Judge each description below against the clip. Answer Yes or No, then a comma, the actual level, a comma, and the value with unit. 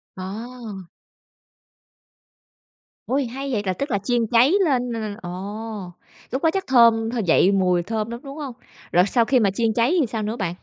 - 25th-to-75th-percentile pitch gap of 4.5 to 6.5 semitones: No, average, 3.9 semitones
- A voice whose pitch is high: Yes, high, 225 Hz